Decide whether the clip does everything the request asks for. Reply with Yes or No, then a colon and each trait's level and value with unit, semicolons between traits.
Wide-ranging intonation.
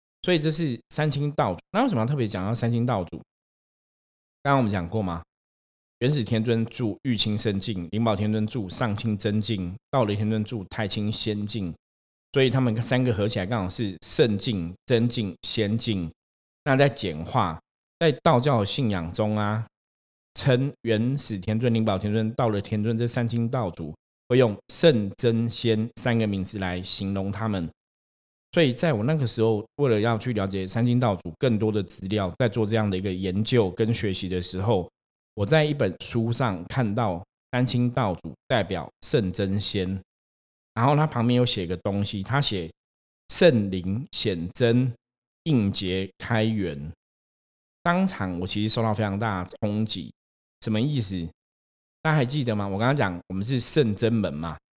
No: average, 4.1 semitones